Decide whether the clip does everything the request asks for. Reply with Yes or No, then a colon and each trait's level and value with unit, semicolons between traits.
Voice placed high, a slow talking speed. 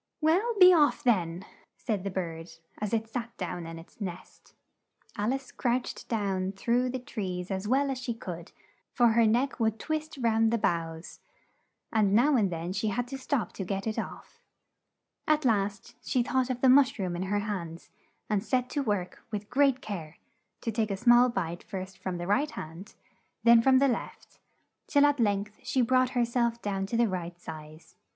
No: high, 220 Hz; average, 190 wpm